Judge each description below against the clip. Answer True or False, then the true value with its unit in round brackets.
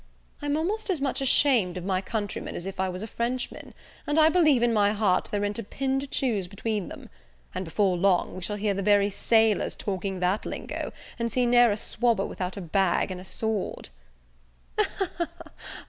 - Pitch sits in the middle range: False (210 Hz)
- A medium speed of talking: True (195 wpm)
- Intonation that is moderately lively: True (4.2 semitones)